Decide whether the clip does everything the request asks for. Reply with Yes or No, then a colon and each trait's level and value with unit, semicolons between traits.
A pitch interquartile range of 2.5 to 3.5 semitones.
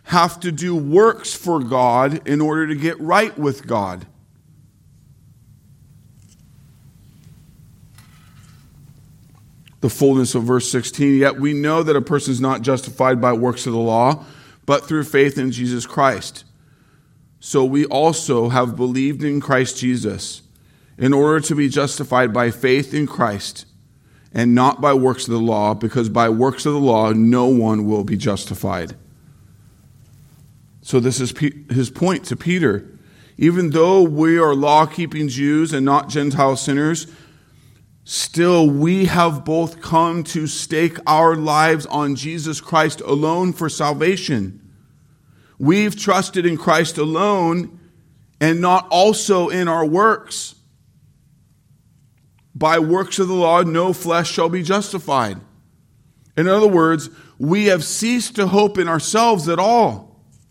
No: average, 4.2 semitones